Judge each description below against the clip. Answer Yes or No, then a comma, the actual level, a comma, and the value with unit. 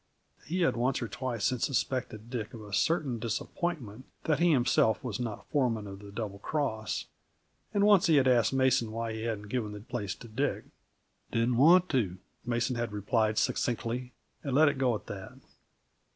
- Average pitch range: Yes, average, 3.6 semitones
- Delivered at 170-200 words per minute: Yes, average, 180 wpm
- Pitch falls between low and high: No, low, 120 Hz